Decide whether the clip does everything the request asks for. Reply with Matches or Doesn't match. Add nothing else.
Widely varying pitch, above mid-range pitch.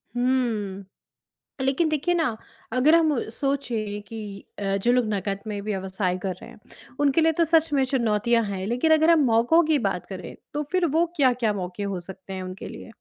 Matches